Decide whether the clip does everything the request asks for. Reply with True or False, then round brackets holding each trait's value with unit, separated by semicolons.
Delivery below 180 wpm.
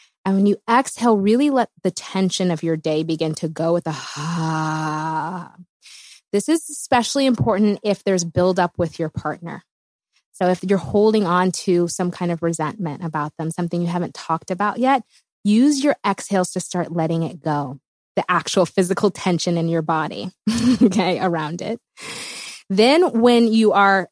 True (170 wpm)